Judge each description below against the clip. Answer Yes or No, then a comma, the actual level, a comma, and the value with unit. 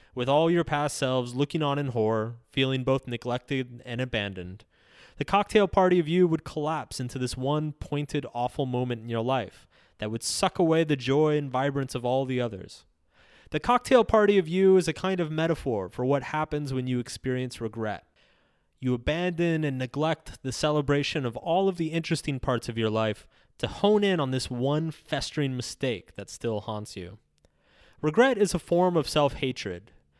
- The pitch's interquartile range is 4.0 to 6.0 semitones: Yes, average, 4.7 semitones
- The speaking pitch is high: No, low, 135 Hz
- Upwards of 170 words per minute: Yes, average, 185 wpm